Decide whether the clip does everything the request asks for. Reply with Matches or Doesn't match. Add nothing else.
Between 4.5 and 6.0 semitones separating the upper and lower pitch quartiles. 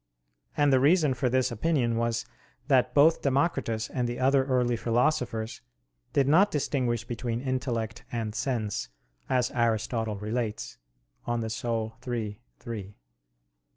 Doesn't match